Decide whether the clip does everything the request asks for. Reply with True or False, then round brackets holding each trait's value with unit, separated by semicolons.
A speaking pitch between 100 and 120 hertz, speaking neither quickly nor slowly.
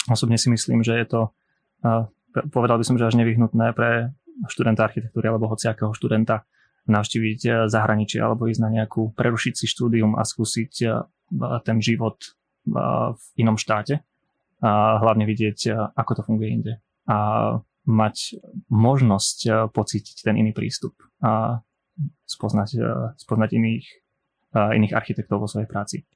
True (115 Hz; 130 wpm)